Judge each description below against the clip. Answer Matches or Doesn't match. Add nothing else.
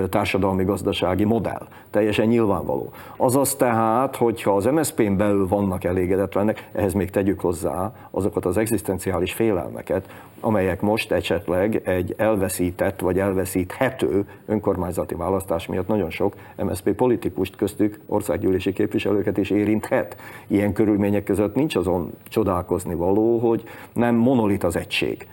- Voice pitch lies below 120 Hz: Matches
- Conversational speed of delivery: Matches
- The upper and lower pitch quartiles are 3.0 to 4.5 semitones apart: Doesn't match